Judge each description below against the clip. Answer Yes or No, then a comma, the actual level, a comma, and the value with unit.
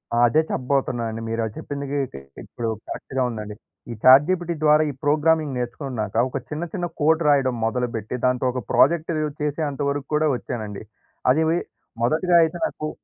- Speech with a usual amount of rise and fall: Yes, average, 4.2 semitones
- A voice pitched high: No, medium, 140 Hz